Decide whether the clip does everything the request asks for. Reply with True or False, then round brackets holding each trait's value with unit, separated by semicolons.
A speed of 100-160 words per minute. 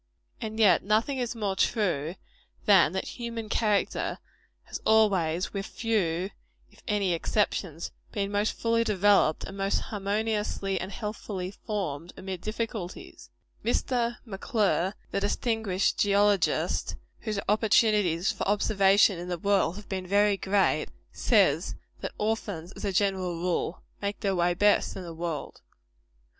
True (135 wpm)